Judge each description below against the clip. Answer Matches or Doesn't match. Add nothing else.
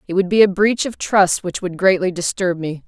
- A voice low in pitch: Doesn't match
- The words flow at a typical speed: Doesn't match